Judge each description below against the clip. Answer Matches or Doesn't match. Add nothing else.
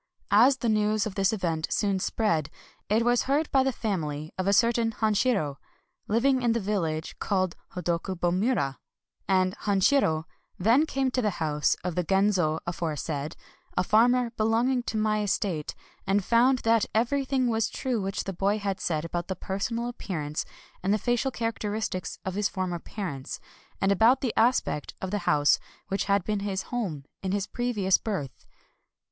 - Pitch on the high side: Matches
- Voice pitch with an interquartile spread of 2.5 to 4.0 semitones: Doesn't match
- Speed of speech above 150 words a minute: Matches